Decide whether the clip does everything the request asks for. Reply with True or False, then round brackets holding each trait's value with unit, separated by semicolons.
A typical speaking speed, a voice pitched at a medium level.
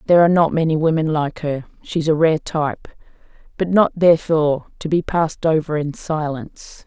True (175 wpm; 155 Hz)